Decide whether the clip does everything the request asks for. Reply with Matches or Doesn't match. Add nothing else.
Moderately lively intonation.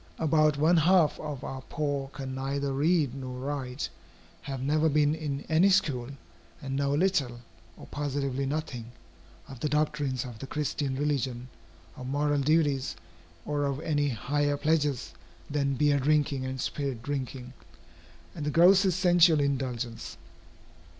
Doesn't match